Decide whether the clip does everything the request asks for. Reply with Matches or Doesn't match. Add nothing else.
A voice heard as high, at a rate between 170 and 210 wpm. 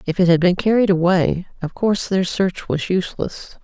Doesn't match